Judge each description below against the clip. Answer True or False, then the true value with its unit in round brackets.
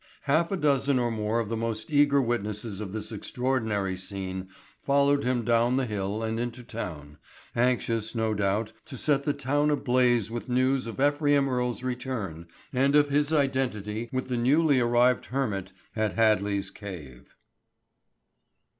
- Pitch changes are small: False (4.1 semitones)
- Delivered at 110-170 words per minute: True (155 wpm)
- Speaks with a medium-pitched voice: False (120 Hz)